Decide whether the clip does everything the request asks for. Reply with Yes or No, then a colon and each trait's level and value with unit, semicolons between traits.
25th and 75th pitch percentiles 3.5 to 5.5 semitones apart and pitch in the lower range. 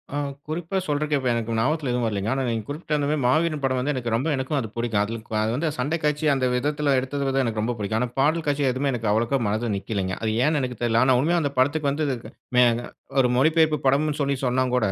Yes: average, 4.1 semitones; low, 130 Hz